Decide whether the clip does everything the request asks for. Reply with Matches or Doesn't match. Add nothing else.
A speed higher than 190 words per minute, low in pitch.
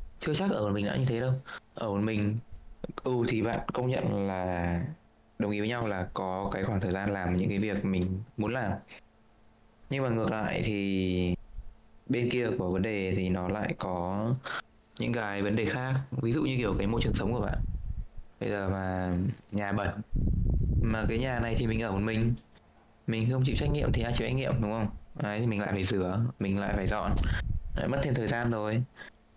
Matches